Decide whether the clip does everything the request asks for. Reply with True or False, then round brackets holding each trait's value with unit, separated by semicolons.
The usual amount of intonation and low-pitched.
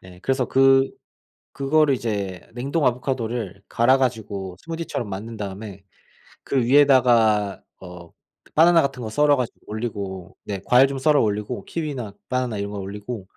True (4.8 semitones; 120 Hz)